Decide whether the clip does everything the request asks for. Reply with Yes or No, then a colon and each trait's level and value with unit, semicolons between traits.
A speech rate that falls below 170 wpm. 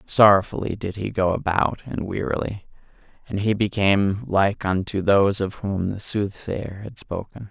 Yes: average, 150 wpm